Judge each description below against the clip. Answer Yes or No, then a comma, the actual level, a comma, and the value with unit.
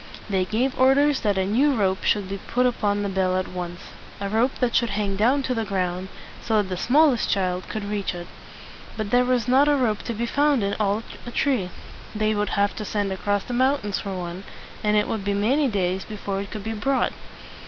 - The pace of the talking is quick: Yes, fast, 220 wpm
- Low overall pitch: No, high, 210 Hz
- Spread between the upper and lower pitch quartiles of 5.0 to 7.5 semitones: No, average, 4.0 semitones